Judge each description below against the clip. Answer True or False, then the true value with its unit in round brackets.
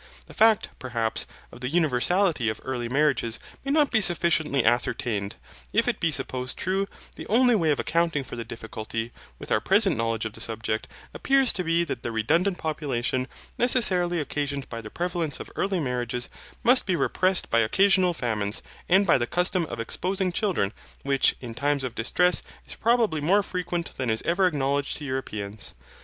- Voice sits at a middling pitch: True (150 Hz)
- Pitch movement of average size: False (7.3 semitones)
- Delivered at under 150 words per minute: False (175 wpm)